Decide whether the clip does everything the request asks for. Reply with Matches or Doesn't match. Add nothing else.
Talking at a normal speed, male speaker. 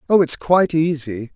Matches